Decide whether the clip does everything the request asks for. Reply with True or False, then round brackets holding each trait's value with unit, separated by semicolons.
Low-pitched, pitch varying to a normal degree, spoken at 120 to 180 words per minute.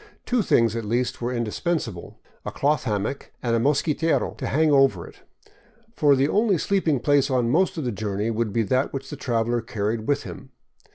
False (125 Hz; 4.2 semitones; 195 wpm)